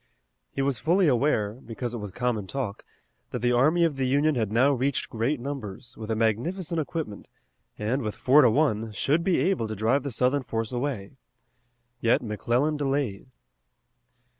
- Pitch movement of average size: Yes, average, 4.4 semitones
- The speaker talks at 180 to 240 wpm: No, average, 170 wpm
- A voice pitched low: Yes, low, 125 Hz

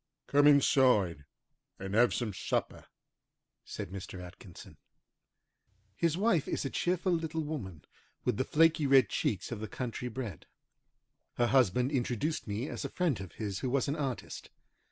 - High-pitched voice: No, low, 125 Hz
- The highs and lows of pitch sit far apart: Yes, wide, 6.4 semitones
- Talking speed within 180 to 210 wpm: No, average, 155 wpm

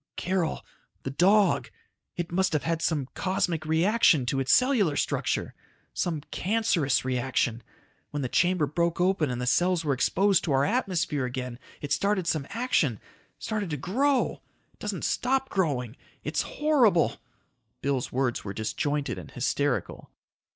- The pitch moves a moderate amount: No, wide, 6.1 semitones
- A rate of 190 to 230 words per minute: No, average, 145 wpm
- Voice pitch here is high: No, medium, 160 Hz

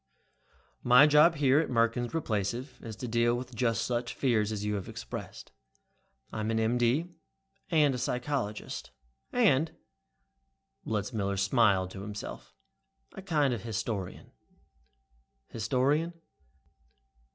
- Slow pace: Yes, slow, 115 wpm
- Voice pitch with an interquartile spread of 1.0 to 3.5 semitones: No, average, 4.0 semitones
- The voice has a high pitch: No, low, 120 Hz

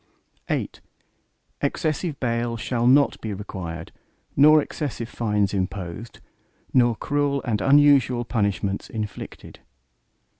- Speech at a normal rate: No, slow, 100 wpm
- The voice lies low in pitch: Yes, low, 115 Hz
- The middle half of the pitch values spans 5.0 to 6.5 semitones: Yes, average, 5.3 semitones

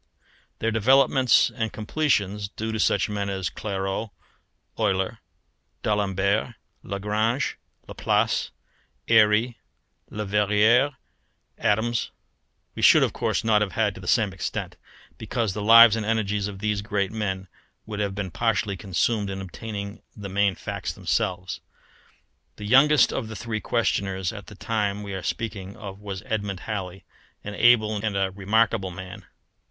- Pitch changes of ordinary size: No, narrow, 2.3 semitones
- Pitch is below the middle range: Yes, low, 105 Hz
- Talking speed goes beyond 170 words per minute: No, average, 140 wpm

